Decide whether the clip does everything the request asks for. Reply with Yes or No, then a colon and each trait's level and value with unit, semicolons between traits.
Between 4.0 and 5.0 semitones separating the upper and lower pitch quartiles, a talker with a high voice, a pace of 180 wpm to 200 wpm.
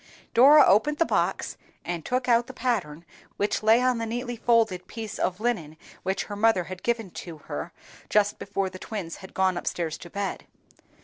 Yes: average, 4.6 semitones; high, 205 Hz; average, 190 wpm